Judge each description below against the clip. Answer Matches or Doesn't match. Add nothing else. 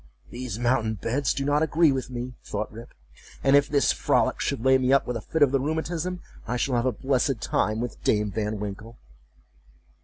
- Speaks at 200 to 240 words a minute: Matches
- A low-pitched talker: Matches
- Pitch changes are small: Doesn't match